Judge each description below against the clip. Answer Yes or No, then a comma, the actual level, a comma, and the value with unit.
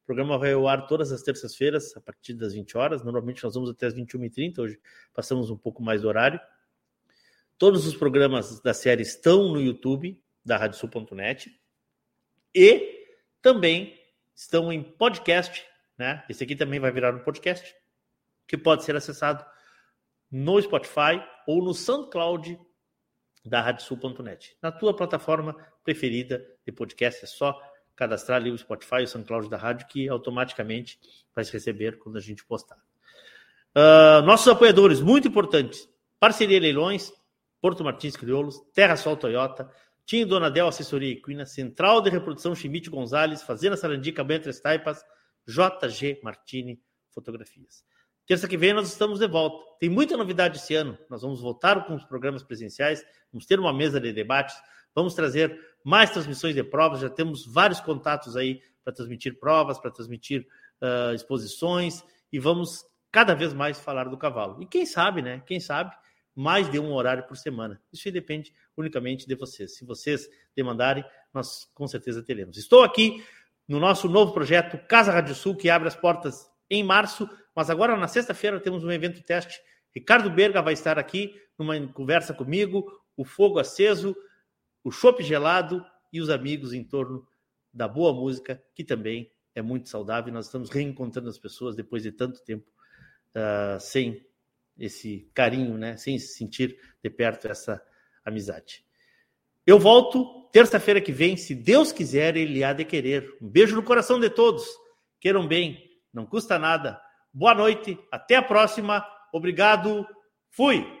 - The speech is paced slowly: No, average, 160 wpm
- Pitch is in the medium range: Yes, medium, 150 Hz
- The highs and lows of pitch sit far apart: Yes, wide, 6.1 semitones